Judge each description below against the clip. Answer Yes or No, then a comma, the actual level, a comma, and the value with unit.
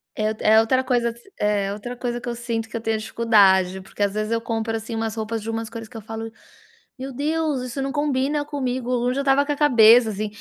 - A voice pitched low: No, high, 230 Hz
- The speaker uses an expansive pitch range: No, average, 2.9 semitones